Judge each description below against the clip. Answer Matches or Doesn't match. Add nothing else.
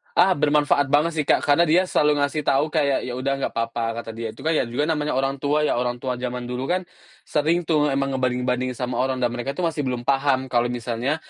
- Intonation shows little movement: Doesn't match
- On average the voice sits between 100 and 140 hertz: Matches